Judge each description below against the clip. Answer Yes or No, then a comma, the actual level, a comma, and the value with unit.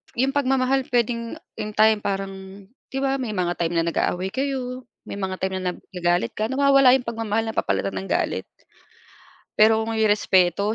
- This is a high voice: Yes, high, 220 Hz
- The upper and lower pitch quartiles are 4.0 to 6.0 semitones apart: Yes, average, 5.0 semitones